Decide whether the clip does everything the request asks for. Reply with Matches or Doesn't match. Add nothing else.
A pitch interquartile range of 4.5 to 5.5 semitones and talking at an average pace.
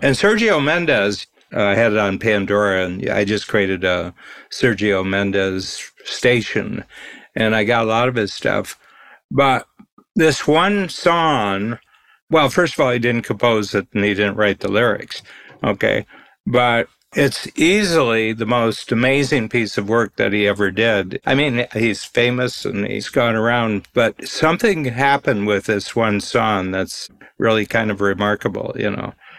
Doesn't match